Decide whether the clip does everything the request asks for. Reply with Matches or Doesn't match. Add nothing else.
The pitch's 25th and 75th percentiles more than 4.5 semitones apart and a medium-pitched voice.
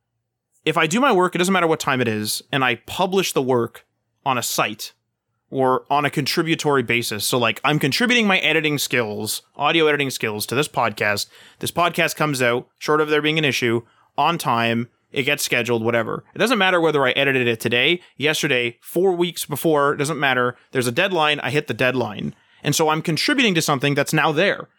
Matches